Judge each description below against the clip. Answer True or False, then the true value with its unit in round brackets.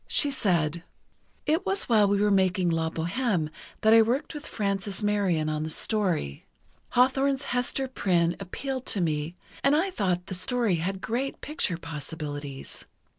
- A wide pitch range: True (6.9 semitones)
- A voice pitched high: True (195 Hz)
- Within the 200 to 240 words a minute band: False (155 wpm)